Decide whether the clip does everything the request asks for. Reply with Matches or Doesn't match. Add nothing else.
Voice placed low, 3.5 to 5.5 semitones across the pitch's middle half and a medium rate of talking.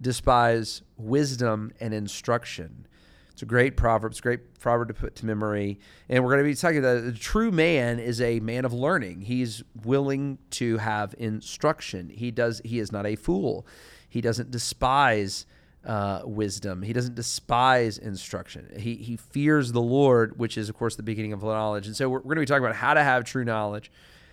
Doesn't match